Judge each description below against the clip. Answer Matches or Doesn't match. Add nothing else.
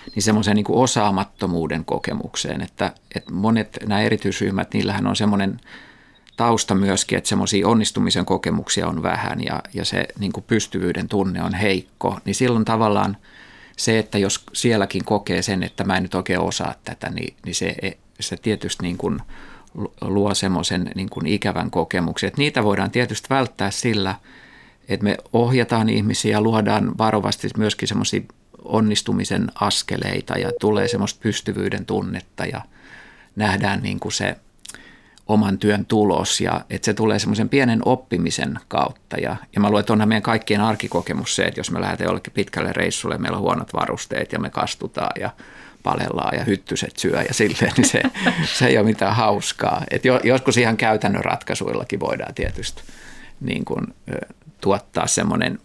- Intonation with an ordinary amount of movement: Doesn't match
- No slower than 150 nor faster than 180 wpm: Matches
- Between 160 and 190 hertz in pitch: Doesn't match